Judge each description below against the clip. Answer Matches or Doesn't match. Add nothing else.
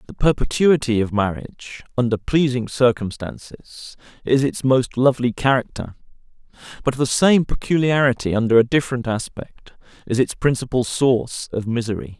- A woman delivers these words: Doesn't match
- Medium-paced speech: Doesn't match